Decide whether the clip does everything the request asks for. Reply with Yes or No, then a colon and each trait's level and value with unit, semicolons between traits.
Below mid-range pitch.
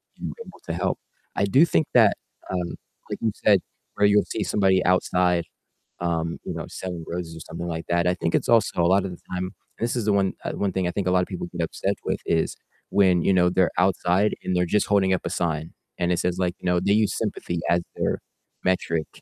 Yes: very low, 90 Hz